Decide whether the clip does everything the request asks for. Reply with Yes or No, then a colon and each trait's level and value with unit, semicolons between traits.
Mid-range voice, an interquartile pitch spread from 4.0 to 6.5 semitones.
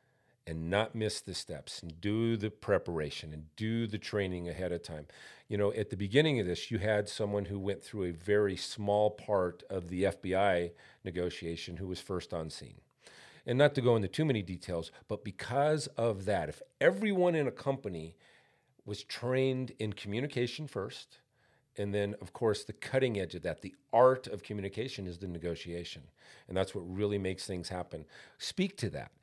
No: low, 100 Hz; average, 4.3 semitones